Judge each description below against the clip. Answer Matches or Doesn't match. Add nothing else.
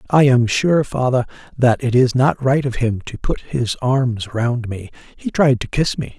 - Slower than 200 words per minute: Doesn't match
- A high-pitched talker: Doesn't match